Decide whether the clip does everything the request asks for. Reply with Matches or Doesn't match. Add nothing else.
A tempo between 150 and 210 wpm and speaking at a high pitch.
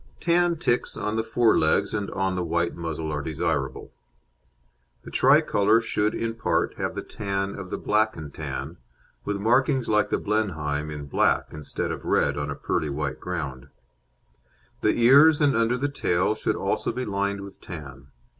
Doesn't match